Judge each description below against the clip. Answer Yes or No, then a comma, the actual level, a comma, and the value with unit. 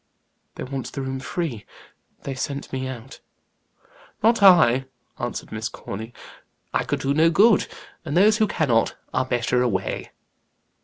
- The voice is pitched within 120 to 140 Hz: Yes, low, 135 Hz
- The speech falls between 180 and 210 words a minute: No, average, 145 wpm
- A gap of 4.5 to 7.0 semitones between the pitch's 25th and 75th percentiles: Yes, average, 5.2 semitones